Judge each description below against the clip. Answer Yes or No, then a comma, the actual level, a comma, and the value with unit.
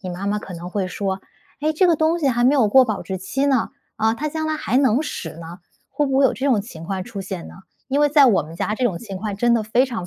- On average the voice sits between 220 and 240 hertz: Yes, high, 225 Hz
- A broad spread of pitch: Yes, wide, 6.1 semitones